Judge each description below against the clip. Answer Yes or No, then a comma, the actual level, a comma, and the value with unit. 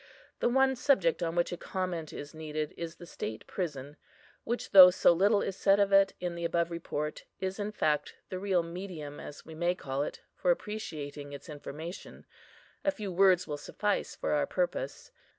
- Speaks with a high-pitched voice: No, medium, 175 Hz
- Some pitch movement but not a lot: Yes, average, 4.3 semitones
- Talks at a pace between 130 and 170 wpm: No, average, 185 wpm